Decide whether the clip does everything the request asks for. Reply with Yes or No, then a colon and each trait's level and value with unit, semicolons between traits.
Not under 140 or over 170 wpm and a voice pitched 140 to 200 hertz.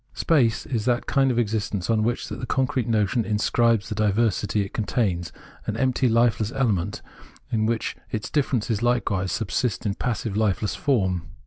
No: average, 160 wpm; low, 110 Hz